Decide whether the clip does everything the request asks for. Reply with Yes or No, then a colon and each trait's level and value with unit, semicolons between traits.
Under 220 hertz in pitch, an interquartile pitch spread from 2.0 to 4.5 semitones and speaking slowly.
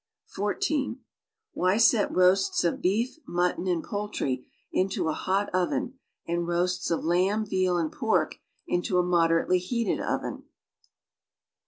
Yes: medium, 185 Hz; average, 2.9 semitones; slow, 130 wpm